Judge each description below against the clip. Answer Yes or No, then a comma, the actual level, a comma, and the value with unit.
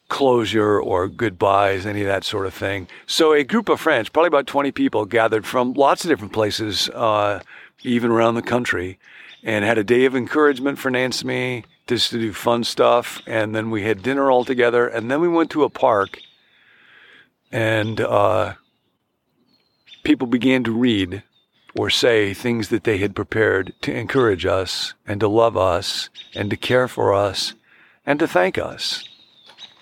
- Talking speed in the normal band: Yes, average, 175 wpm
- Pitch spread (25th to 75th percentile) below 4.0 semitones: Yes, average, 3.1 semitones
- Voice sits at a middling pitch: No, low, 115 Hz